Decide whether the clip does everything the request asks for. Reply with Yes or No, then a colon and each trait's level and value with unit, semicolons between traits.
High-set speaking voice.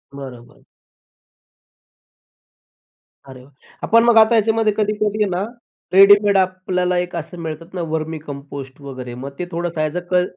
No: medium, 175 Hz